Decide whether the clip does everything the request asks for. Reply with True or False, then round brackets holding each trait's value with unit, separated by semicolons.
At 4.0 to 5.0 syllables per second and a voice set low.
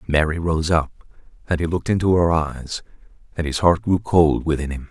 False (5.5 syllables/s; 80 Hz)